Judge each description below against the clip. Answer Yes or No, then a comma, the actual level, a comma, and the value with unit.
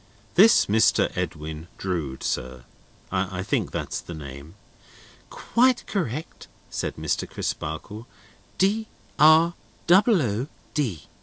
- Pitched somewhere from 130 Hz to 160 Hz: No, low, 110 Hz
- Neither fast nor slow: No, slow, 105 wpm